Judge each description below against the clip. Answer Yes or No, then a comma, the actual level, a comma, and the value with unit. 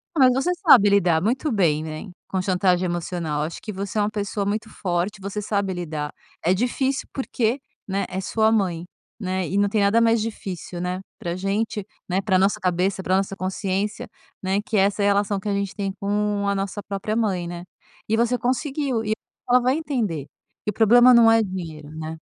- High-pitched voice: Yes, high, 200 Hz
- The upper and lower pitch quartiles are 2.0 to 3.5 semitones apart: Yes, average, 3.1 semitones